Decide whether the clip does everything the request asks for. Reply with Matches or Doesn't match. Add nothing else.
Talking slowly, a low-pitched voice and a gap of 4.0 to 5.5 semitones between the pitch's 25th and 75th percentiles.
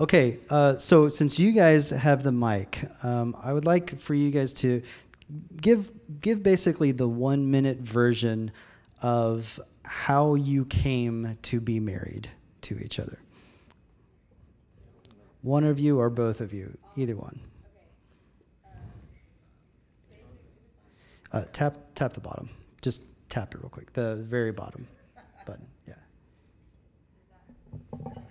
Matches